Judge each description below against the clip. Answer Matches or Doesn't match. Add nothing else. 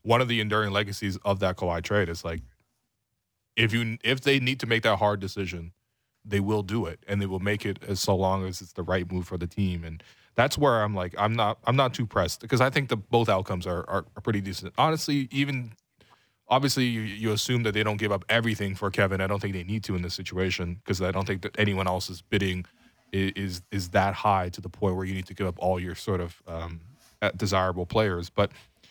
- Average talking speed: Doesn't match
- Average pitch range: Matches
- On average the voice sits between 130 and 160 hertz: Doesn't match